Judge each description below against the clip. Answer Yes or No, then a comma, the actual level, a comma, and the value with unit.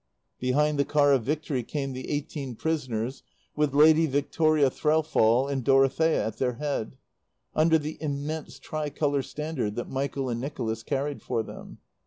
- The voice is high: No, medium, 140 Hz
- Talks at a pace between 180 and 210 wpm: No, average, 150 wpm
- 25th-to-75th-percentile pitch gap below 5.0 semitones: Yes, average, 2.8 semitones